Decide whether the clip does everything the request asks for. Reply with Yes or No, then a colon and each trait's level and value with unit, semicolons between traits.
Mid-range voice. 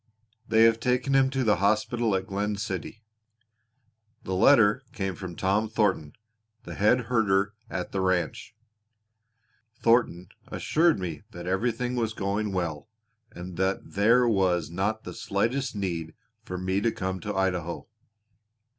No: low, 100 Hz